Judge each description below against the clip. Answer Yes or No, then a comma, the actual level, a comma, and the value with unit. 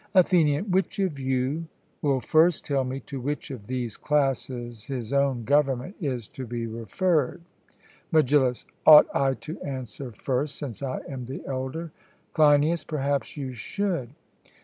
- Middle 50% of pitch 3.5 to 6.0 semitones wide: No, average, 3.1 semitones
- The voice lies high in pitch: No, low, 135 Hz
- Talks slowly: No, average, 145 wpm